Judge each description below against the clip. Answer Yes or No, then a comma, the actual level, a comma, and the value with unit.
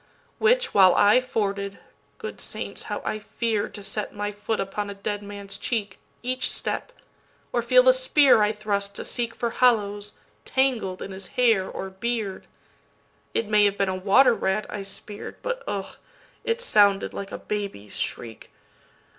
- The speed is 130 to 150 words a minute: Yes, average, 145 wpm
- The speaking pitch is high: Yes, high, 205 Hz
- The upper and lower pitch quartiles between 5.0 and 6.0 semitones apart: No, average, 3.2 semitones